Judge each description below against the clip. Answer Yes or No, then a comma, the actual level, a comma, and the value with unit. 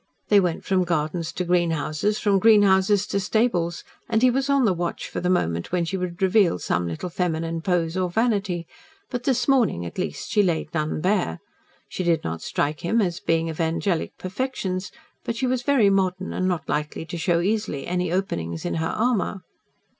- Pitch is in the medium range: Yes, medium, 180 Hz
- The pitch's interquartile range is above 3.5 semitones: Yes, average, 3.9 semitones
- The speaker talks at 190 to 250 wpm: Yes, average, 195 wpm